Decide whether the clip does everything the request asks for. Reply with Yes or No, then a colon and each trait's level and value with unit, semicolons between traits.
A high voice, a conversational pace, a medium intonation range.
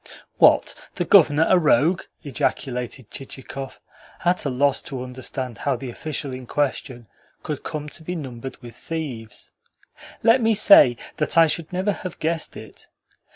No: medium, 145 Hz; average, 155 wpm; average, 4.5 semitones